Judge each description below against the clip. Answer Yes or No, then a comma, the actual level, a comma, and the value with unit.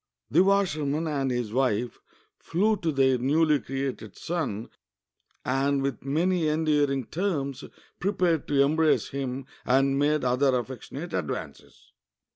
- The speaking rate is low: Yes, slow, 125 wpm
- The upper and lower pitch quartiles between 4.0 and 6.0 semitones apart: No, average, 3.3 semitones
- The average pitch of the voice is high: No, medium, 140 Hz